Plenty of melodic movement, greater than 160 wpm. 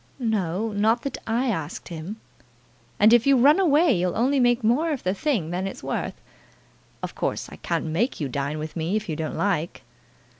Yes: wide, 6.7 semitones; average, 195 wpm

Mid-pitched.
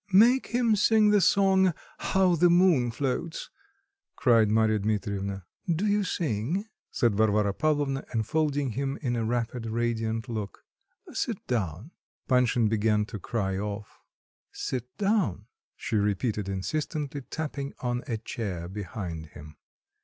No: low, 120 Hz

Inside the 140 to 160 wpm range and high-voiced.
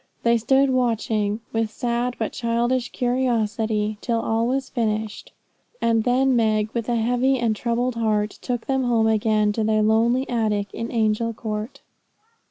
Yes: average, 155 wpm; high, 230 Hz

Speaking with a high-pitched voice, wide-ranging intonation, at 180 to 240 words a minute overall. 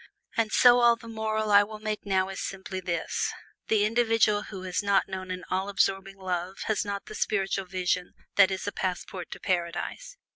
No: high, 195 Hz; narrow, 2.4 semitones; average, 190 wpm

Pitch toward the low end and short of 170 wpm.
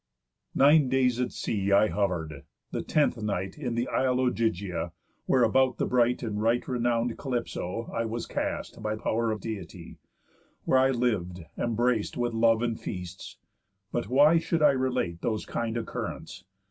Yes: low, 115 Hz; average, 160 wpm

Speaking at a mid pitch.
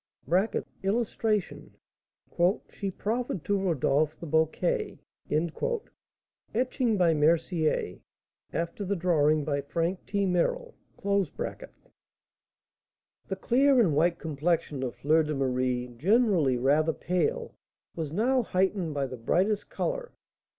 Yes: medium, 170 Hz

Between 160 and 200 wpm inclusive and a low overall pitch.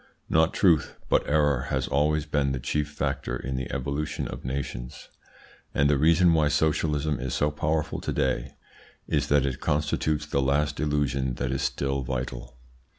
Yes: average, 165 wpm; very low, 70 Hz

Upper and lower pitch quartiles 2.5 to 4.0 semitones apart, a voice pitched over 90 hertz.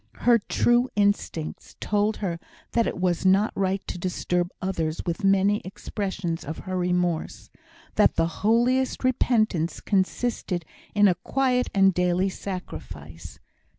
Yes: average, 3.3 semitones; high, 190 Hz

